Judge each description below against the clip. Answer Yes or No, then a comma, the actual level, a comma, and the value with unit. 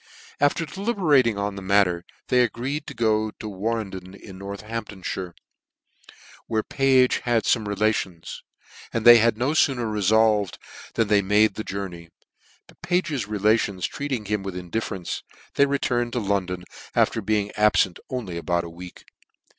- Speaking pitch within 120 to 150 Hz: No, low, 105 Hz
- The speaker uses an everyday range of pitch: Yes, average, 3.6 semitones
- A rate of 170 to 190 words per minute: No, average, 150 wpm